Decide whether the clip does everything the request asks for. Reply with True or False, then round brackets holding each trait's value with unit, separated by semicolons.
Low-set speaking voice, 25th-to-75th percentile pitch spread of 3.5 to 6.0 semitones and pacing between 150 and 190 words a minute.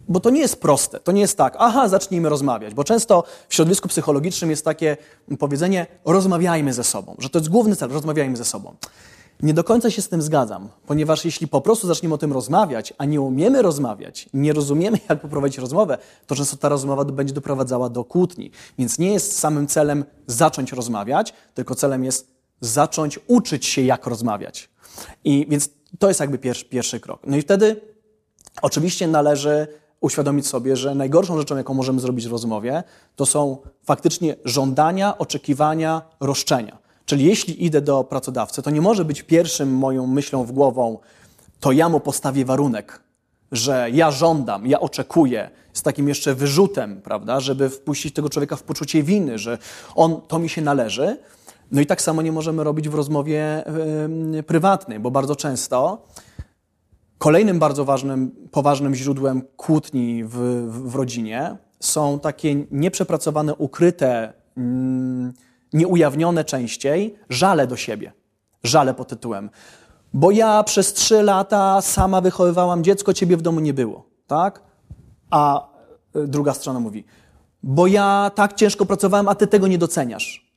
False (150 Hz; 4.3 semitones; 160 wpm)